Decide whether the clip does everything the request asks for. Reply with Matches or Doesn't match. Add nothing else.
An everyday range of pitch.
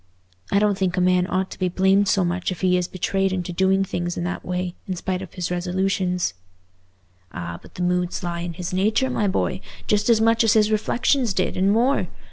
Doesn't match